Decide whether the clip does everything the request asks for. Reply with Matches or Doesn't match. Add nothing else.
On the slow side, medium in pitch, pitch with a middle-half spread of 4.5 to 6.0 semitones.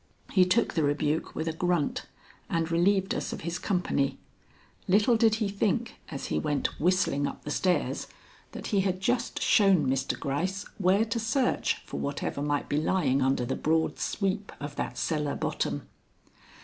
Doesn't match